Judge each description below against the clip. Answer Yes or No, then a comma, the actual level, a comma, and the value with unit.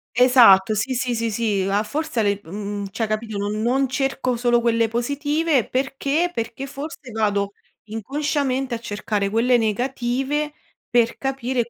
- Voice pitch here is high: Yes, high, 240 Hz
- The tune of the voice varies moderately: Yes, average, 3.9 semitones